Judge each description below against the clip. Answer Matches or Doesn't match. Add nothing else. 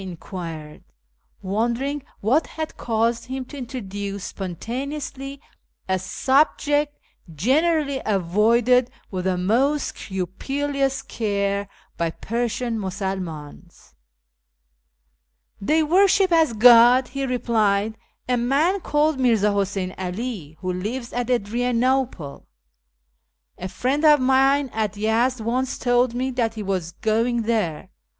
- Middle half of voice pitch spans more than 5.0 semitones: Matches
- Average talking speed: Doesn't match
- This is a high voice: Matches